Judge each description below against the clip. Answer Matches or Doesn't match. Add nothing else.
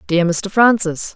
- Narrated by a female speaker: Matches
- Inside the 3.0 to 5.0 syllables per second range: Matches